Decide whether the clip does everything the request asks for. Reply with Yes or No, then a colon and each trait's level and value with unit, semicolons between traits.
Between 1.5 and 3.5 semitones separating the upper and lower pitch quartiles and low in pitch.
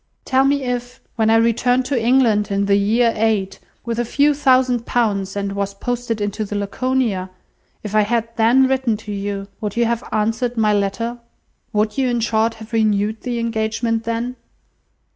No: average, 2.7 semitones; high, 225 Hz